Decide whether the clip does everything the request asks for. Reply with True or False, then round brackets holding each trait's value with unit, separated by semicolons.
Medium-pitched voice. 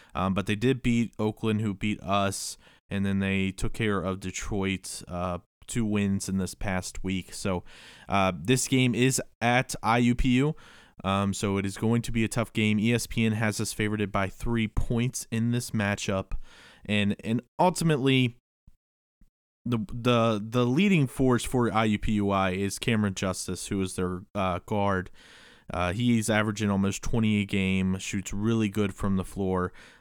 False (105 Hz)